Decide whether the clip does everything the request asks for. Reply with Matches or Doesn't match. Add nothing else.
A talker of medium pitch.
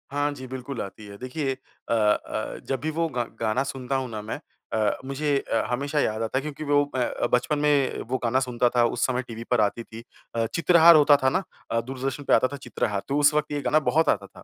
Doesn't match